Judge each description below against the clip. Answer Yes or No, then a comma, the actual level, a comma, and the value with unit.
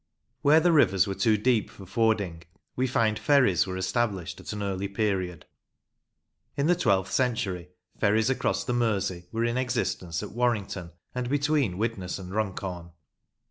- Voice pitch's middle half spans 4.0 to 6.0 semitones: Yes, average, 4.6 semitones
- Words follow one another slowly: No, average, 155 wpm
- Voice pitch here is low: Yes, low, 105 Hz